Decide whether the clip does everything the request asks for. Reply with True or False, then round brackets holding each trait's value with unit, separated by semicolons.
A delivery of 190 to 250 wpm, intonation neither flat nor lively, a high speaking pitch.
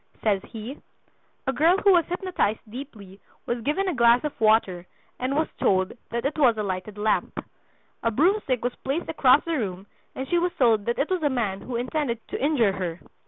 False (200 wpm; 6.1 semitones; 245 Hz)